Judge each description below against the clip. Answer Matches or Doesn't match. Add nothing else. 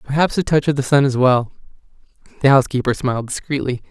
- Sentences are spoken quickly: Doesn't match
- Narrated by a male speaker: Matches